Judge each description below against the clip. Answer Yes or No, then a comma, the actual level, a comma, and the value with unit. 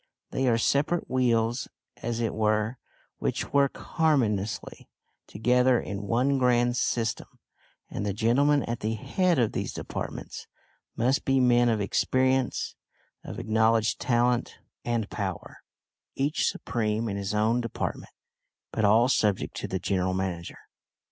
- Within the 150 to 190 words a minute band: No, slow, 135 wpm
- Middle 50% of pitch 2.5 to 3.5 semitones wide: Yes, average, 3.0 semitones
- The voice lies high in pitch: No, low, 115 Hz